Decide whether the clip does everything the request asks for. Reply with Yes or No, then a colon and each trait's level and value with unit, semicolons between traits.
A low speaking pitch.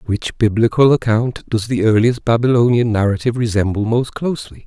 Yes: low, 115 Hz